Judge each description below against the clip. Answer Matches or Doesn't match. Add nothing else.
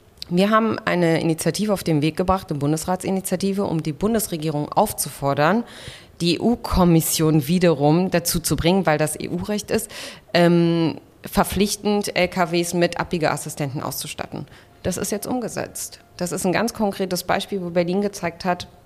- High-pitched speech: Doesn't match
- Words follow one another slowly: Doesn't match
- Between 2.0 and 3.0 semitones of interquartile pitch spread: Doesn't match